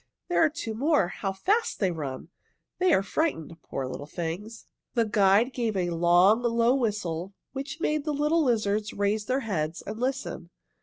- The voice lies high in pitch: Yes, high, 215 Hz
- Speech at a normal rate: Yes, average, 170 wpm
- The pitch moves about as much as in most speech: No, wide, 6.8 semitones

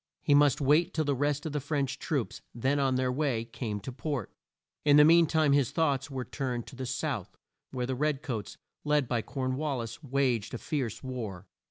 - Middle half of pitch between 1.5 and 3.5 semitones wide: Yes, average, 2.8 semitones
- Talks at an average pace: No, fast, 210 wpm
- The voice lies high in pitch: No, low, 135 Hz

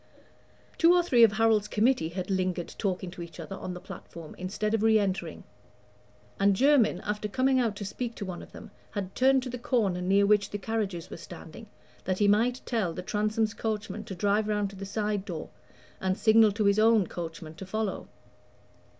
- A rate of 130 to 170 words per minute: No, average, 200 wpm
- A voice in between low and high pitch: No, high, 205 Hz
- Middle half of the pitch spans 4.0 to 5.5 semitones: No, average, 2.9 semitones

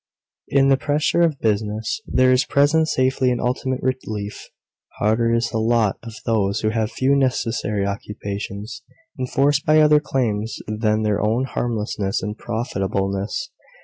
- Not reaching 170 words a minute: Yes, average, 145 wpm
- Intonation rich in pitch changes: No, average, 3.9 semitones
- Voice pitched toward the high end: No, low, 115 Hz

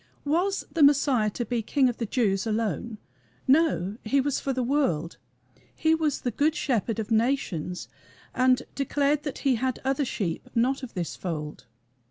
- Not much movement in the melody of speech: No, average, 4.7 semitones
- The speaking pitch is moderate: No, very high, 255 Hz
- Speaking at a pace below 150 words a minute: No, average, 175 wpm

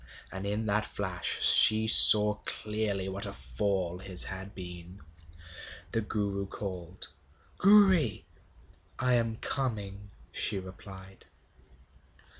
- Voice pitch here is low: Yes, low, 100 Hz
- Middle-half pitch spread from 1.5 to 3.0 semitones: Yes, narrow, 2.5 semitones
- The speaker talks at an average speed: No, slow, 105 wpm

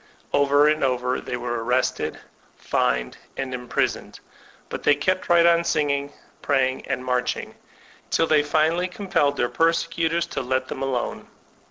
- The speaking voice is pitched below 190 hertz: Yes, medium, 140 Hz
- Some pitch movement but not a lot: Yes, average, 4.3 semitones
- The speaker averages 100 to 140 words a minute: No, average, 150 wpm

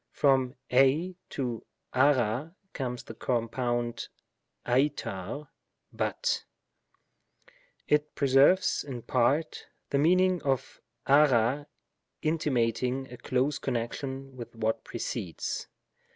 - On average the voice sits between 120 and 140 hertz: Yes, low, 135 Hz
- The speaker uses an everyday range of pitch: Yes, average, 3.5 semitones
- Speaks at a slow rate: Yes, slow, 95 wpm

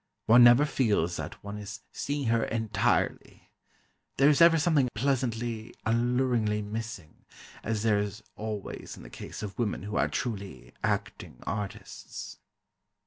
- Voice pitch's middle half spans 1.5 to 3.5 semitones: Yes, average, 3.1 semitones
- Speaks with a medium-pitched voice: No, low, 110 Hz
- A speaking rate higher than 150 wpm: No, average, 140 wpm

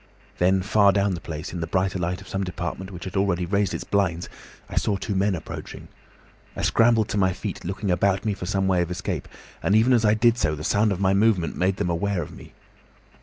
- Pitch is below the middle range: Yes, very low, 95 Hz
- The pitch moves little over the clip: Yes, narrow, 2.3 semitones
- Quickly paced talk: Yes, fast, 235 wpm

